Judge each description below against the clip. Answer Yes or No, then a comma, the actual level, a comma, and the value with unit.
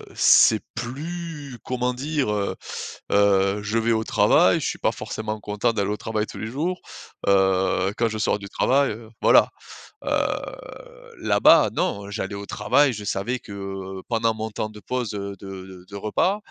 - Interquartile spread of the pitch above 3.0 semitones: Yes, average, 3.7 semitones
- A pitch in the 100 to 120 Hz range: Yes, low, 110 Hz